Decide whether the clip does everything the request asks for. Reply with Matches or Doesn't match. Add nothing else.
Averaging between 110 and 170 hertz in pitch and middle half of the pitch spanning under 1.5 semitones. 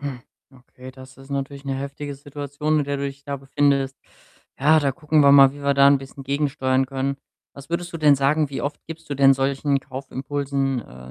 Matches